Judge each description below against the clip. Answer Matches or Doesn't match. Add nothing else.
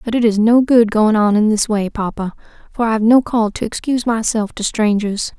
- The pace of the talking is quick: Matches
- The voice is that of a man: Doesn't match